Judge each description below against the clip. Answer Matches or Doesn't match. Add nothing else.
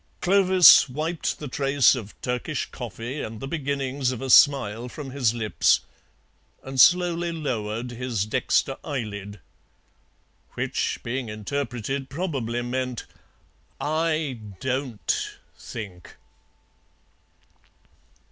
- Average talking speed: Doesn't match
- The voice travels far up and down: Doesn't match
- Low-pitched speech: Matches